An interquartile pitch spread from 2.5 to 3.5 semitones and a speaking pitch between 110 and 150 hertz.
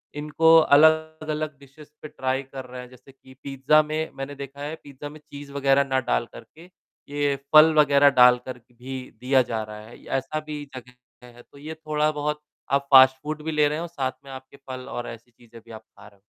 Yes: average, 2.8 semitones; medium, 140 Hz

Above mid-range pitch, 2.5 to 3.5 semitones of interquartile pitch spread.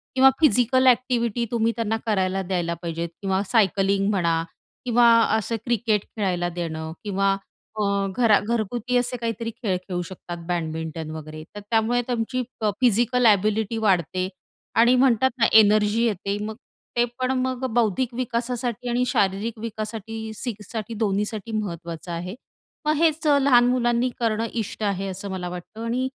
No: high, 220 Hz; average, 3.9 semitones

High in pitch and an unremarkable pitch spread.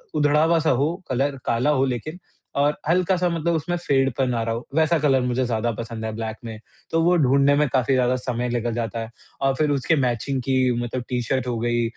No: low, 130 Hz; average, 3.9 semitones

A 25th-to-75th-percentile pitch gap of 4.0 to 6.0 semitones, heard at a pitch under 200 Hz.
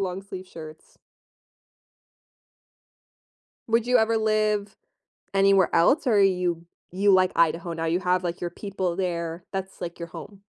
No: average, 2.8 semitones; medium, 185 Hz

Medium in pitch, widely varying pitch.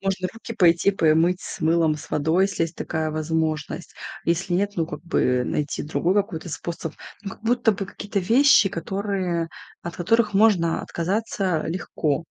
No: medium, 175 Hz; average, 3.6 semitones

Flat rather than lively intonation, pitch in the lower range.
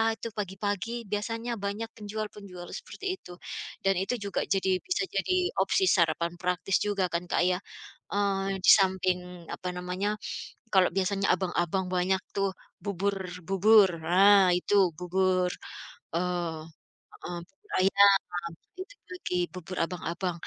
No: narrow, 2.0 semitones; high, 190 Hz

